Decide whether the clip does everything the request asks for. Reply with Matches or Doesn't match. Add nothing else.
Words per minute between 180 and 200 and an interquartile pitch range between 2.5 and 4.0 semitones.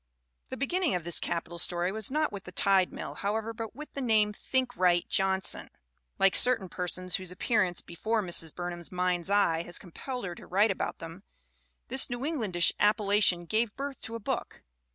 Doesn't match